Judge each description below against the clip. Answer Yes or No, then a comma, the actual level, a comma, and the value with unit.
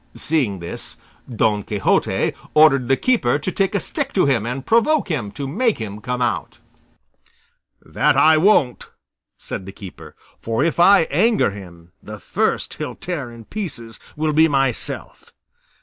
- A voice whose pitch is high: No, low, 135 Hz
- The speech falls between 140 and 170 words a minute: Yes, average, 155 wpm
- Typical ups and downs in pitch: No, wide, 7.4 semitones